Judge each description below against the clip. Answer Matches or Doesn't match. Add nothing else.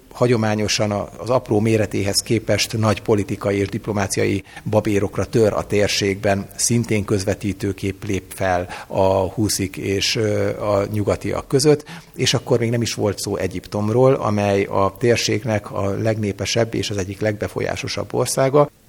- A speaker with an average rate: Matches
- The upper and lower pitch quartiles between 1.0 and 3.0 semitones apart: Matches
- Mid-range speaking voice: Doesn't match